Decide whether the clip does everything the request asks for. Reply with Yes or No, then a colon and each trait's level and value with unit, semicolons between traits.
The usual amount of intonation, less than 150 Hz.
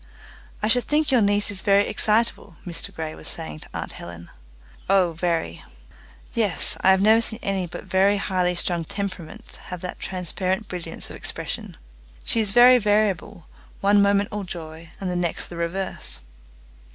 No: average, 3.2 semitones; high, 190 Hz